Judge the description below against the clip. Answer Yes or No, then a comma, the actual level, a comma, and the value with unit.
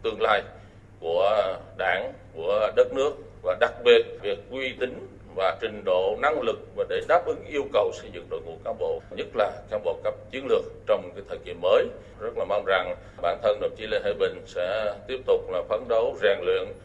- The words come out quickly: No, average, 215 wpm